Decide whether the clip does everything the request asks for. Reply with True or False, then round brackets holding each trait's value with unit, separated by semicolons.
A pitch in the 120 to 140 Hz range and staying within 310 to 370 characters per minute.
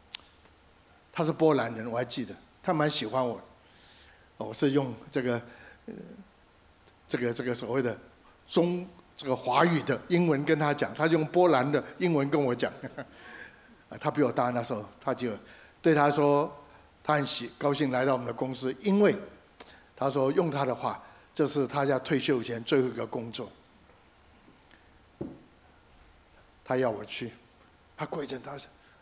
False (135 Hz; 205 characters per minute)